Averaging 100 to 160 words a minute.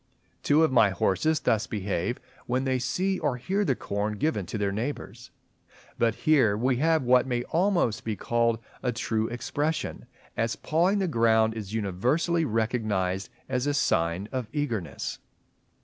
Yes: average, 155 wpm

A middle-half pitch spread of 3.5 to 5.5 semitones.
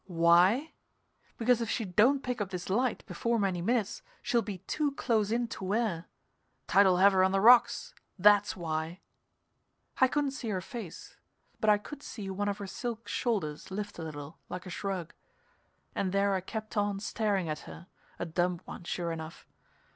Yes: average, 4.3 semitones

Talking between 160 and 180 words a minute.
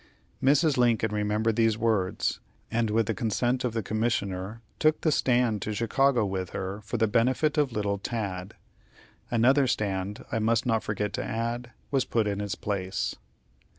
Yes: average, 165 wpm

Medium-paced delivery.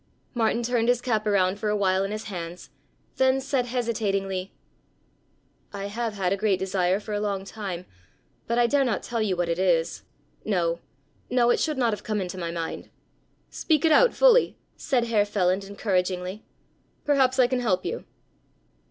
Yes: average, 180 wpm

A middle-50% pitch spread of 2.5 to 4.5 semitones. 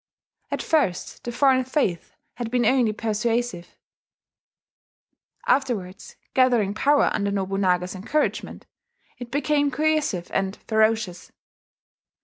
No: average, 5.2 semitones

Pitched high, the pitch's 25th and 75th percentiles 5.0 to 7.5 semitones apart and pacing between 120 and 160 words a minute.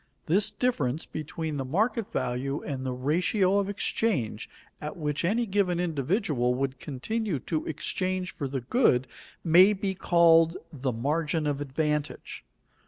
No: medium, 160 Hz; wide, 5.4 semitones; average, 140 wpm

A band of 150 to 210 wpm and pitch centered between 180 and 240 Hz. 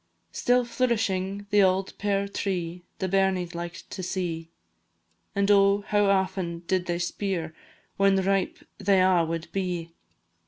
No: average, 140 wpm; high, 190 Hz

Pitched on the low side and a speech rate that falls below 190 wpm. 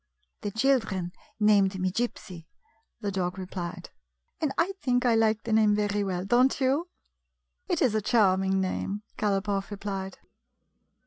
No: high, 205 Hz; average, 155 wpm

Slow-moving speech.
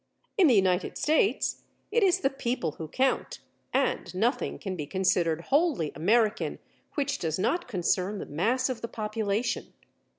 No: average, 155 wpm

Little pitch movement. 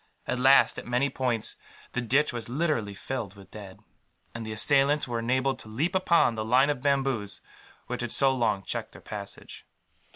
No: average, 3.8 semitones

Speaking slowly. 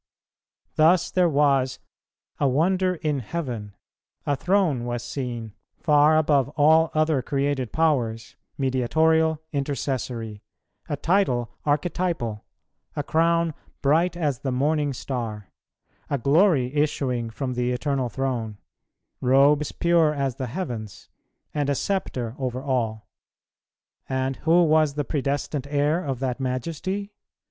Yes: slow, 120 wpm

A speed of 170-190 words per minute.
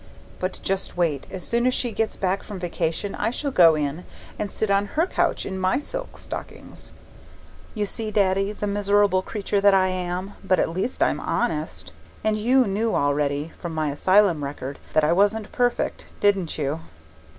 Yes: average, 180 wpm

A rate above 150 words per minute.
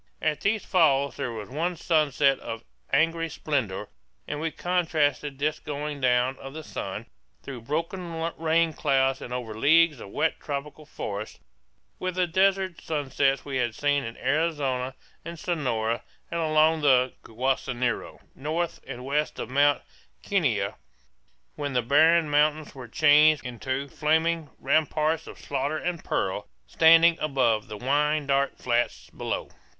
No: average, 145 wpm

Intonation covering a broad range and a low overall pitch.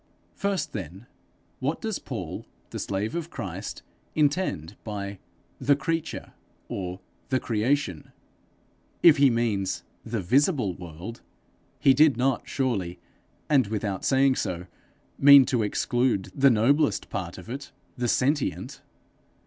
Yes: wide, 6.0 semitones; low, 120 Hz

